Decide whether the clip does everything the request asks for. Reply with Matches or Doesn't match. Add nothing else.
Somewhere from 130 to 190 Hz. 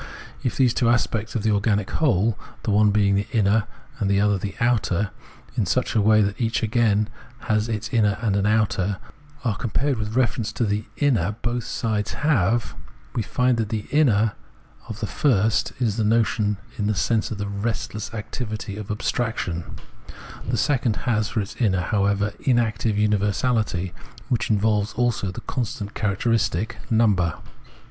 Doesn't match